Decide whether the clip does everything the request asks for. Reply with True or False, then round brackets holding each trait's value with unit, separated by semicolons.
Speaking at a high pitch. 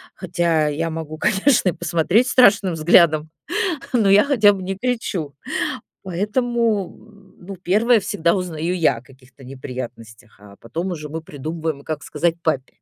False (170 Hz)